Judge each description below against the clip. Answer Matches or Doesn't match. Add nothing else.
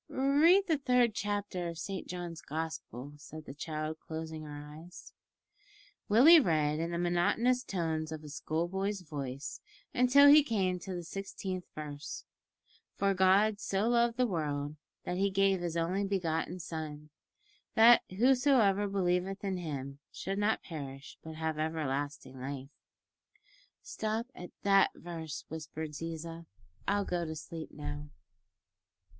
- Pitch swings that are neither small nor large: Matches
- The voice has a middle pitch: Matches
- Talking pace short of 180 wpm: Matches